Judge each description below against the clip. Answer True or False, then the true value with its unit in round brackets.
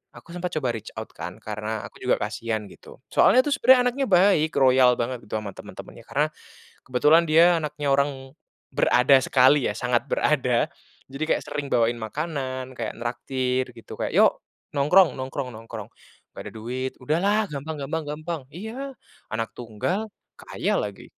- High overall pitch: False (135 Hz)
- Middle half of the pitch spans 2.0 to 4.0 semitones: False (4.9 semitones)